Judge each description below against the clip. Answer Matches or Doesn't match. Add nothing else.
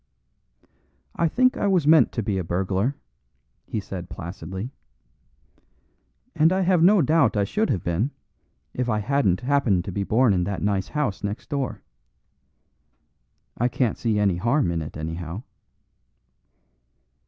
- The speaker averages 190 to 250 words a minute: Doesn't match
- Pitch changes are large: Matches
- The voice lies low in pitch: Matches